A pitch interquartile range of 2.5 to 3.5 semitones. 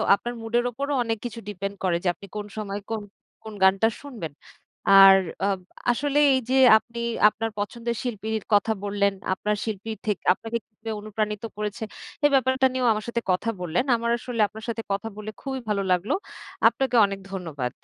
Yes: average, 2.8 semitones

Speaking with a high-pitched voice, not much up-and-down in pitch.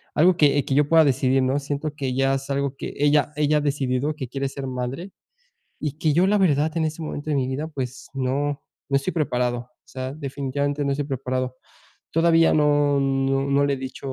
No: medium, 140 Hz; narrow, 2.1 semitones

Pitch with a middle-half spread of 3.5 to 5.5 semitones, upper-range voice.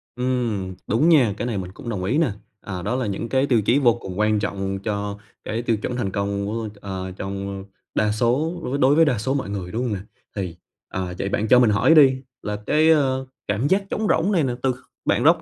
No: average, 4.8 semitones; low, 115 Hz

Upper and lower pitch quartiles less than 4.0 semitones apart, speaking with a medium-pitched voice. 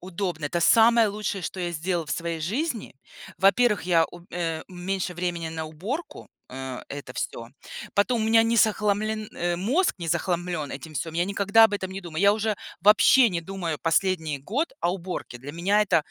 No: average, 4.3 semitones; medium, 180 Hz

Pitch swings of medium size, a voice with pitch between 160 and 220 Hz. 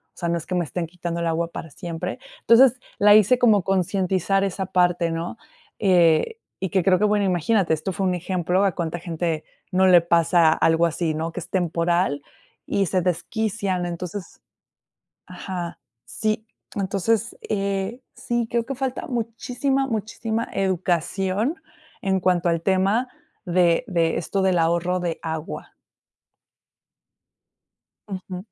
Yes: average, 3.1 semitones; medium, 185 Hz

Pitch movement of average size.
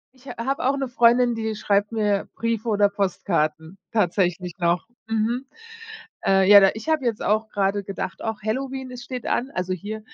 Yes: average, 3.7 semitones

